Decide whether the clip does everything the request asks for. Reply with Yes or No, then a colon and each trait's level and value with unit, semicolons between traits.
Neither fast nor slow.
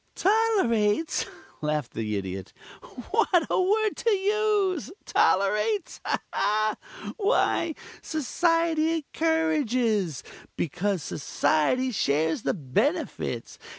No: slow, 80 wpm